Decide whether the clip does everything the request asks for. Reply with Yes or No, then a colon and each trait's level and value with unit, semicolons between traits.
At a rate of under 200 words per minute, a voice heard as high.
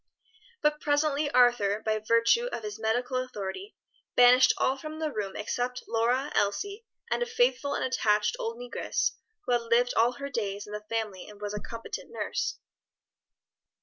Yes: average, 165 wpm; high, 245 Hz